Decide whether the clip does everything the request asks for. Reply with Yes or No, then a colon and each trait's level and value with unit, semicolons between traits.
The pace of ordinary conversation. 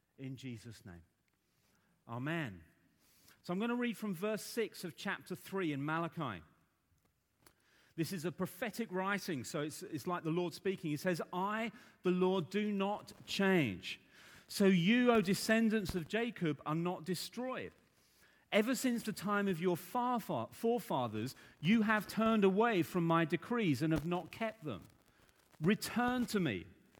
Yes: average, 155 wpm